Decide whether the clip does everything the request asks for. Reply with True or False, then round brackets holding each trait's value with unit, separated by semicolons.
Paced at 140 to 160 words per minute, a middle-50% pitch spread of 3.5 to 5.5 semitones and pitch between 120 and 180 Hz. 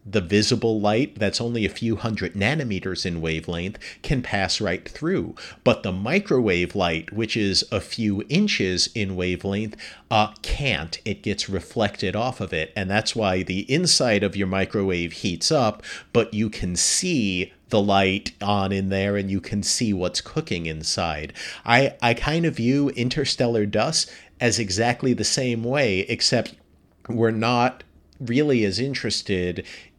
False (155 wpm; 3.8 semitones; 105 Hz)